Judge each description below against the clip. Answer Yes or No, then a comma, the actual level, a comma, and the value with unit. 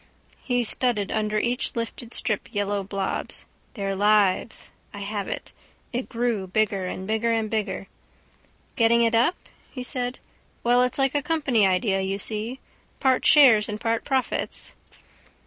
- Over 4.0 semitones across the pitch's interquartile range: No, average, 3.3 semitones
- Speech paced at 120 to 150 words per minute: Yes, average, 145 wpm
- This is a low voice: No, high, 225 Hz